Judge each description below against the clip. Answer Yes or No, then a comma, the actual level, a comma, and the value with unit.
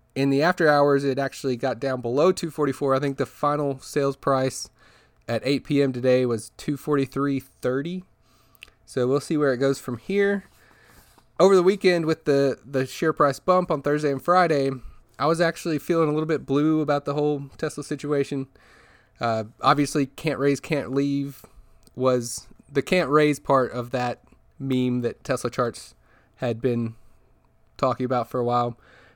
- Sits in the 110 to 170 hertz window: Yes, medium, 140 Hz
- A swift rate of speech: No, average, 165 wpm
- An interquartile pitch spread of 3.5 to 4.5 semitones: No, average, 2.8 semitones